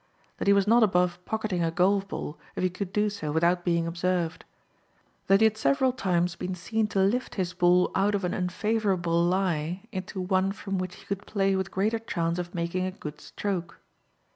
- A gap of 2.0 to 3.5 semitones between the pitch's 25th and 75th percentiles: Yes, narrow, 2.4 semitones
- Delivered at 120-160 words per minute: No, average, 200 wpm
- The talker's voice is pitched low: No, medium, 185 Hz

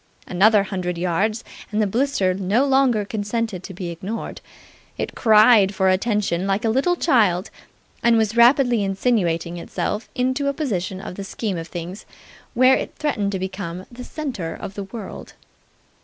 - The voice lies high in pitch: Yes, high, 205 Hz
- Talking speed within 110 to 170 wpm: Yes, average, 160 wpm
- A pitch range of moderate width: Yes, average, 4.2 semitones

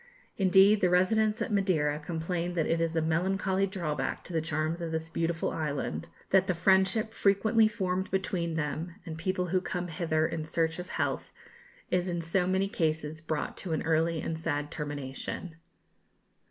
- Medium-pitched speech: Yes, medium, 170 Hz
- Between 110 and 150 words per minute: No, average, 170 wpm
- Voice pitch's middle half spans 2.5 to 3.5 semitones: Yes, average, 2.9 semitones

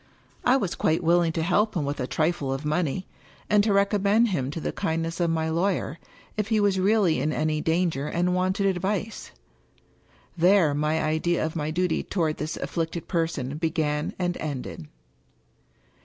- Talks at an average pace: Yes, average, 170 wpm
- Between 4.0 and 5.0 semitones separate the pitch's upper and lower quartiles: No, average, 3.5 semitones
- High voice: No, medium, 170 Hz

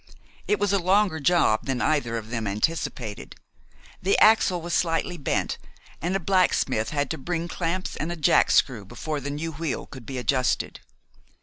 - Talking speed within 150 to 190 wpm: Yes, average, 170 wpm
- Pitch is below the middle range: No, medium, 160 Hz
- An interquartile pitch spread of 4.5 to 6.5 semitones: Yes, wide, 5.5 semitones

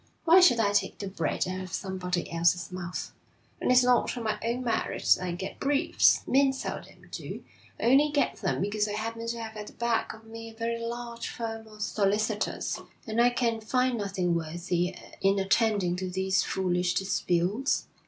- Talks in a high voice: Yes, high, 215 Hz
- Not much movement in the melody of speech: No, average, 4.0 semitones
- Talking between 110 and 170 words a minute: No, average, 190 wpm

